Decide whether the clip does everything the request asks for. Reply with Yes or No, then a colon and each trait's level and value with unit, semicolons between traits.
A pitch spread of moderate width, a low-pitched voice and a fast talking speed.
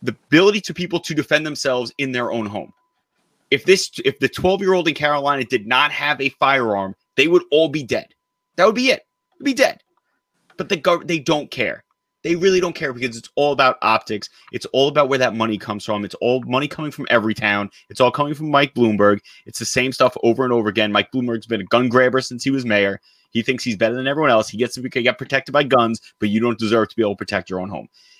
Yes: average, 4.8 semitones; low, 130 Hz; fast, 250 wpm